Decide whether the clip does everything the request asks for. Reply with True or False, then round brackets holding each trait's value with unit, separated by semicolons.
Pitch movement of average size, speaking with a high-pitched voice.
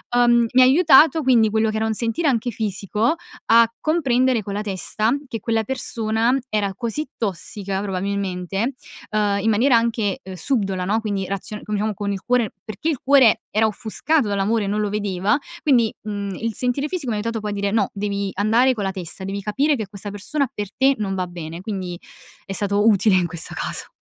True (3.2 semitones; 215 Hz)